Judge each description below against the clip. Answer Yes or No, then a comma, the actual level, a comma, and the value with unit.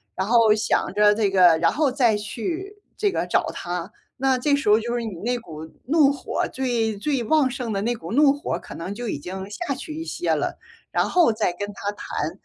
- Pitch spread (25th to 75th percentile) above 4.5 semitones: Yes, wide, 5.4 semitones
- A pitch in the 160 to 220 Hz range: No, high, 230 Hz